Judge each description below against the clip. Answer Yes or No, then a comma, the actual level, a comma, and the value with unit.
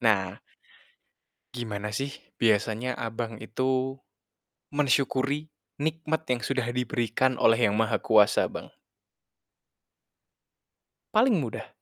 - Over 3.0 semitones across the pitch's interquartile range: Yes, average, 3.7 semitones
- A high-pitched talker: No, low, 125 Hz